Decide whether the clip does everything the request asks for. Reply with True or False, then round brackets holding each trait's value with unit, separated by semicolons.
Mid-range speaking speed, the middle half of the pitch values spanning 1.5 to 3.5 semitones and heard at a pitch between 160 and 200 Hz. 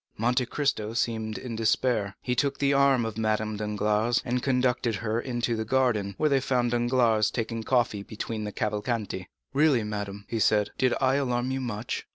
False (180 wpm; 2.9 semitones; 115 Hz)